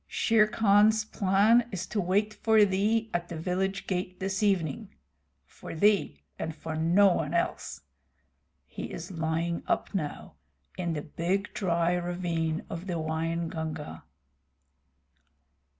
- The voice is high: No, medium, 180 Hz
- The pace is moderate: No, slow, 130 wpm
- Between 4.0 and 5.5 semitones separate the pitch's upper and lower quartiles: No, average, 3.6 semitones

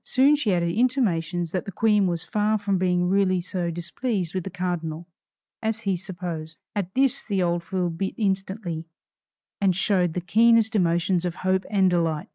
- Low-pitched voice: No, medium, 185 Hz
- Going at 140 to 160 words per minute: No, average, 175 wpm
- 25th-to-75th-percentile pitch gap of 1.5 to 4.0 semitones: Yes, average, 3.0 semitones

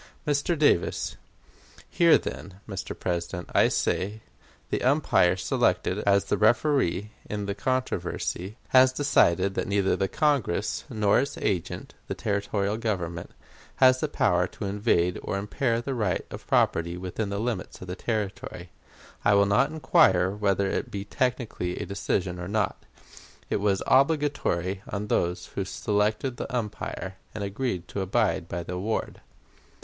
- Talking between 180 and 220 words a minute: No, average, 150 wpm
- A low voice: Yes, low, 100 Hz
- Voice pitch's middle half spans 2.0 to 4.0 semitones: No, average, 4.7 semitones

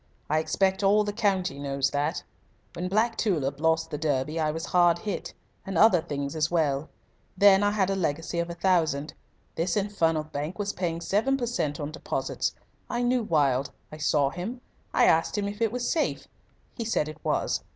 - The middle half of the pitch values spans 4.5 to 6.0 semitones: Yes, average, 5.1 semitones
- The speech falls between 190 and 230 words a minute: Yes, average, 195 wpm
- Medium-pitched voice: Yes, medium, 170 Hz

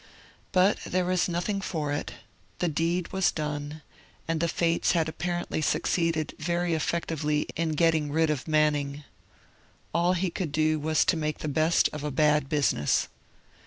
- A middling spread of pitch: No, narrow, 2.3 semitones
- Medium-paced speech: Yes, average, 160 wpm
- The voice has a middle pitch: Yes, medium, 160 Hz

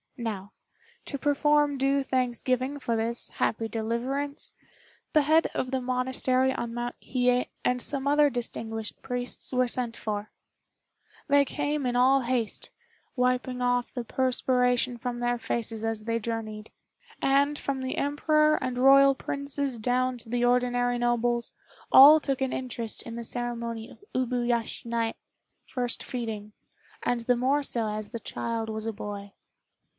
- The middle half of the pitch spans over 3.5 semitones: No, narrow, 2.4 semitones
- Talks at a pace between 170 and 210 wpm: No, average, 150 wpm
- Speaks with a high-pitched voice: Yes, high, 245 Hz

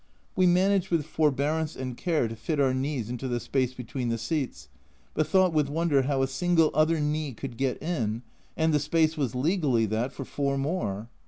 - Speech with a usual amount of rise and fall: Yes, average, 4.1 semitones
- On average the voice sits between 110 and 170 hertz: Yes, medium, 140 Hz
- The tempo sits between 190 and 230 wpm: Yes, average, 195 wpm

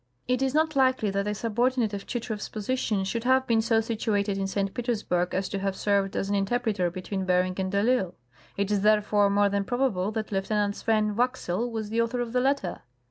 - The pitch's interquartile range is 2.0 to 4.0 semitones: Yes, average, 3.5 semitones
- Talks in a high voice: Yes, high, 210 Hz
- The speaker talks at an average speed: No, fast, 210 wpm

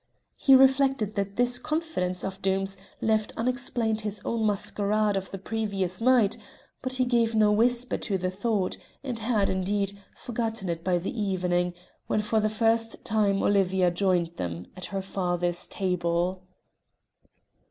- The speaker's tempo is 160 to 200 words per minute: No, average, 145 wpm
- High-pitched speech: Yes, high, 205 Hz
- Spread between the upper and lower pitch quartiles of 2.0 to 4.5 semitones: Yes, average, 3.4 semitones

